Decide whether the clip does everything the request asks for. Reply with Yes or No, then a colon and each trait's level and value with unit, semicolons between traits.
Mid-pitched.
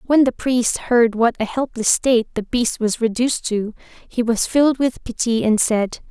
No: high, 235 Hz